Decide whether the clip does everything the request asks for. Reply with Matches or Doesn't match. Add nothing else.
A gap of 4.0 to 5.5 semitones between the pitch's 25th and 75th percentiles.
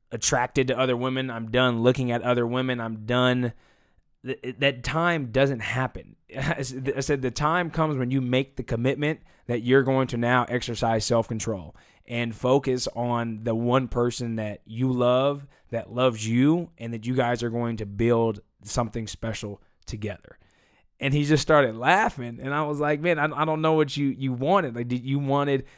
Doesn't match